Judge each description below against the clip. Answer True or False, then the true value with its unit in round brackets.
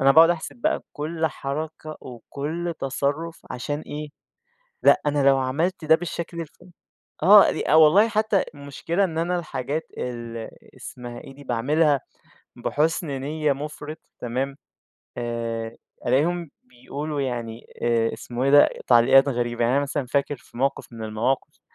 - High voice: False (140 Hz)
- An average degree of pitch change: True (4.4 semitones)